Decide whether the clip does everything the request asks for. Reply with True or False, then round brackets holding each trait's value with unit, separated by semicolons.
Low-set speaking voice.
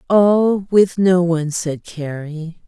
False (175 Hz)